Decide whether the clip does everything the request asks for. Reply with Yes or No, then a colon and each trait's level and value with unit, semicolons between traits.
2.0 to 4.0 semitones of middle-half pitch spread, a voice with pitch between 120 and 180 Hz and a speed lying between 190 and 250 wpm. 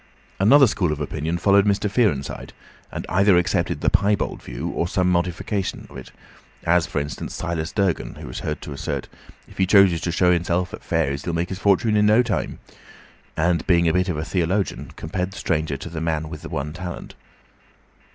No: average, 3.5 semitones; very low, 90 Hz; average, 200 wpm